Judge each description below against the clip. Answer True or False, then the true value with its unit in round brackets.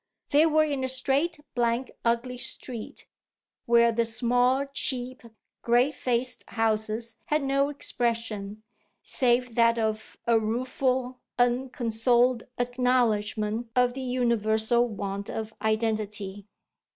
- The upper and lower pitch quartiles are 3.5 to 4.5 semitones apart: False (2.4 semitones)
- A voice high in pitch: True (240 Hz)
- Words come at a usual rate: False (110 wpm)